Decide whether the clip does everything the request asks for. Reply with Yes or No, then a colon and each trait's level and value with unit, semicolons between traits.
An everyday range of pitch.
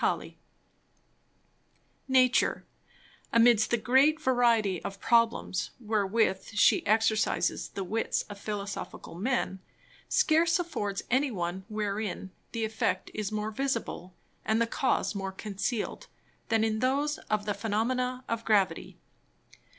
Yes: average, 3.6 semitones